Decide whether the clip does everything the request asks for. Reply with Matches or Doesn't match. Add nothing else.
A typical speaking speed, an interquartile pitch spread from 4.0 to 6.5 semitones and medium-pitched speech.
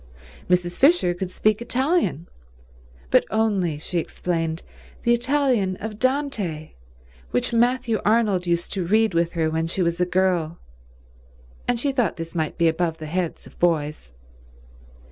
Matches